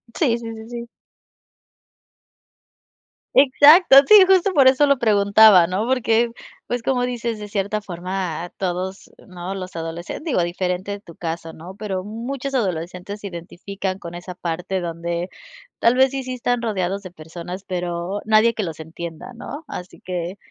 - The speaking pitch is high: Yes, high, 195 Hz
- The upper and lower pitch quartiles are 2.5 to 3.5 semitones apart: No, average, 5.1 semitones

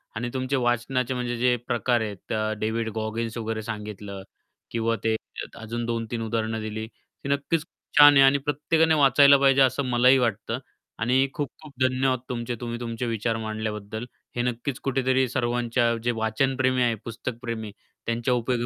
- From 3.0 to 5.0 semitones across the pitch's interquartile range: No, narrow, 2.6 semitones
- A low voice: Yes, low, 120 Hz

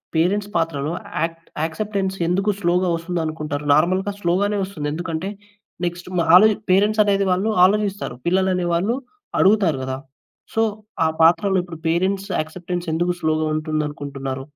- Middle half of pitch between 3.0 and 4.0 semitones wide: Yes, average, 3.4 semitones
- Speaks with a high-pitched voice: No, medium, 175 Hz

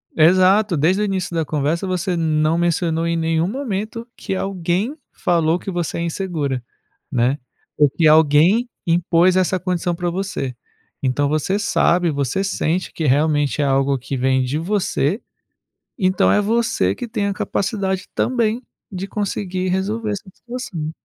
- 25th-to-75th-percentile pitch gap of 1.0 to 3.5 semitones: No, average, 4.0 semitones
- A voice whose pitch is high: No, medium, 175 Hz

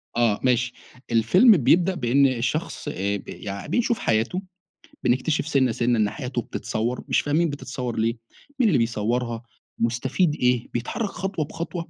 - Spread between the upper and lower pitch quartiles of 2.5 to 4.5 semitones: No, wide, 5.5 semitones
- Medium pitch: No, low, 125 Hz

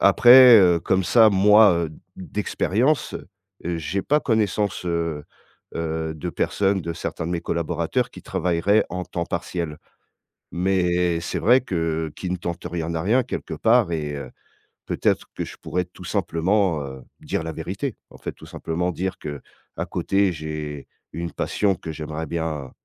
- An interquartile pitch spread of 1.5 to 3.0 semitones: No, average, 3.5 semitones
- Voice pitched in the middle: No, very low, 85 Hz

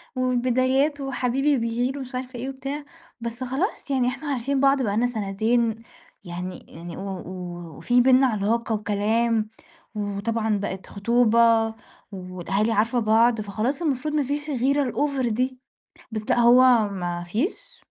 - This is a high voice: Yes, high, 240 Hz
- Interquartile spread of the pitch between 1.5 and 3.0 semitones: No, average, 3.7 semitones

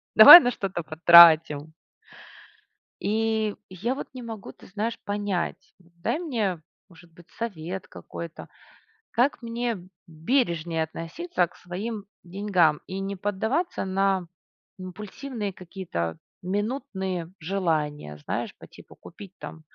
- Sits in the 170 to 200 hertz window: Yes, high, 190 Hz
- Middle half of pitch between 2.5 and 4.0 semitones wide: No, average, 4.5 semitones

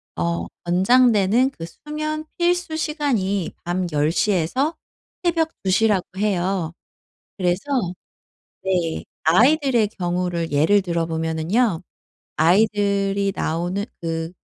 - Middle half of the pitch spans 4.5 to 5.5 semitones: No, wide, 6.2 semitones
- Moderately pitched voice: No, high, 195 Hz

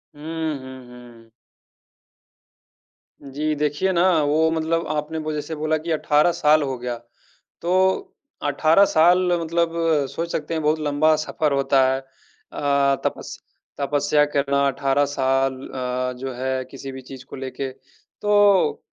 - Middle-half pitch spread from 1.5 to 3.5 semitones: Yes, average, 3.2 semitones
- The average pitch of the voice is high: No, medium, 150 Hz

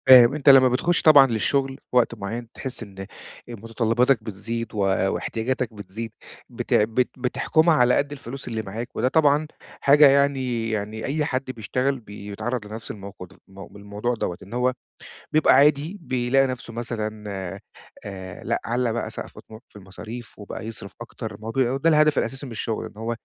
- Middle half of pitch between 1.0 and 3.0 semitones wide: No, average, 3.7 semitones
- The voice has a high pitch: No, low, 120 Hz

